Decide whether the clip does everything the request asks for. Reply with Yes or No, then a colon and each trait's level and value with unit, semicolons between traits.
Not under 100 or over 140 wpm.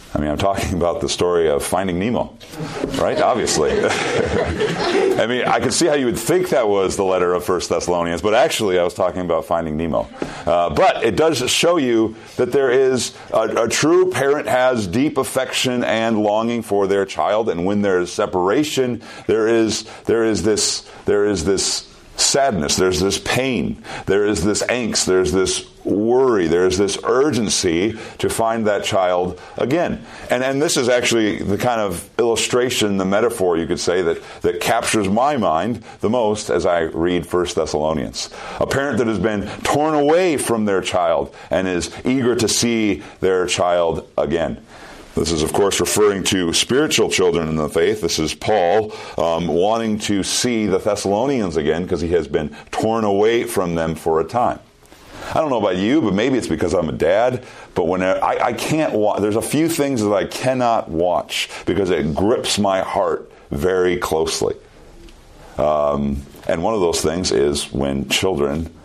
No: average, 180 wpm